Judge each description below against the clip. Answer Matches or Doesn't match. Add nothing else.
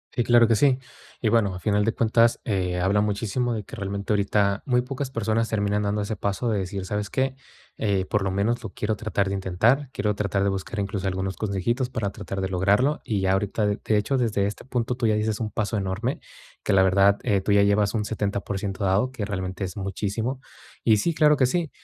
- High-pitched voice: Doesn't match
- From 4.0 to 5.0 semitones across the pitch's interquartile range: Doesn't match